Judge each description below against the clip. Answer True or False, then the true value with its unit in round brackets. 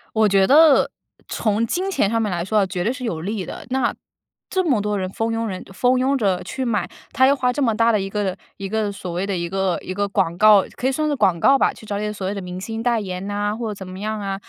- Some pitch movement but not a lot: True (3.4 semitones)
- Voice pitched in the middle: False (210 Hz)